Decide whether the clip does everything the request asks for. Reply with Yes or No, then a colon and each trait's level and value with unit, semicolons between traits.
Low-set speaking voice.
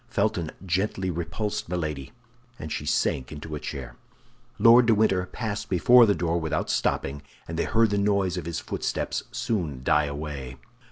Yes: very low, 90 Hz